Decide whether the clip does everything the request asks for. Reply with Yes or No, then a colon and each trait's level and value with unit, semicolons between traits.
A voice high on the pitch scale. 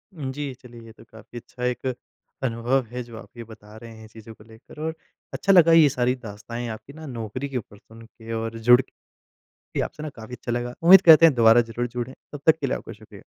No: low, 120 Hz